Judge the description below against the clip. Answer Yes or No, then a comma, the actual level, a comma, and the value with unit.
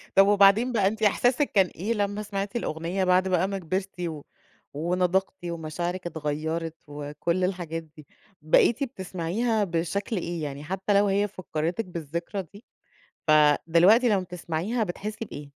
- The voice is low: No, medium, 180 Hz